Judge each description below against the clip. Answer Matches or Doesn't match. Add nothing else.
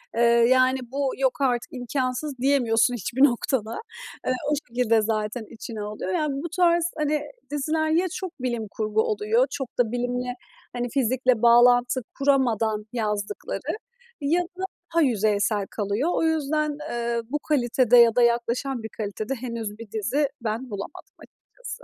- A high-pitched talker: Matches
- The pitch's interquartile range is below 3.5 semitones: Doesn't match